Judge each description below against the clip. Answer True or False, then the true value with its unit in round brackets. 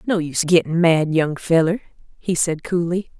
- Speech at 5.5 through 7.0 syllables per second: False (4.9 syllables/s)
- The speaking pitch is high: False (170 Hz)